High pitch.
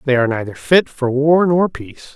No: medium, 145 Hz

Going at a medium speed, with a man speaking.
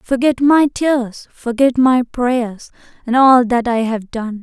No: average, 165 wpm; female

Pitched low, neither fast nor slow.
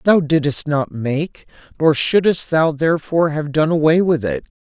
No: medium, 155 Hz; average, 170 wpm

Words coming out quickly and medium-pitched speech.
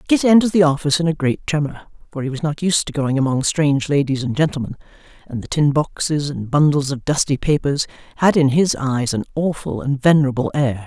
Yes: fast, 210 wpm; medium, 145 Hz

